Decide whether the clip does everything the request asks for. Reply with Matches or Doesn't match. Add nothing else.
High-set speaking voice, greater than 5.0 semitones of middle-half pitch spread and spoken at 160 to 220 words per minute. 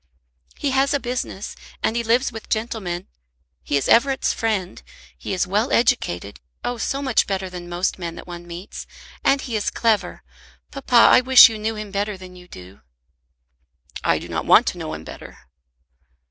Matches